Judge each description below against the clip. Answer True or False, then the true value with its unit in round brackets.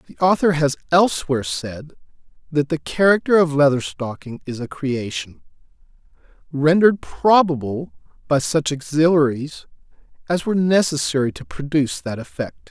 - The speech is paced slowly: True (125 wpm)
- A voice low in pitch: False (145 Hz)